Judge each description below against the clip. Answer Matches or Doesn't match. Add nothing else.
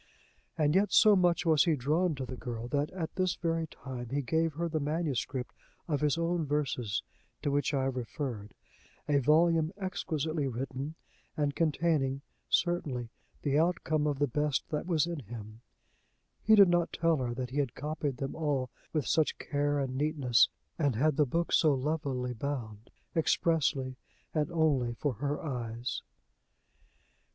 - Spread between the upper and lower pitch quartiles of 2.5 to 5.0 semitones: Matches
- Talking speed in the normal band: Matches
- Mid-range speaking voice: Matches